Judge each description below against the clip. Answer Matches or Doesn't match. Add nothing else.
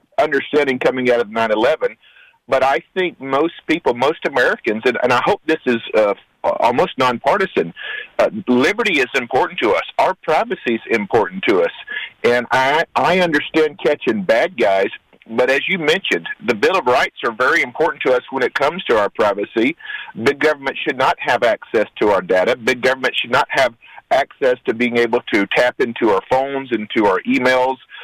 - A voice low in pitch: Doesn't match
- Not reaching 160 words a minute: Doesn't match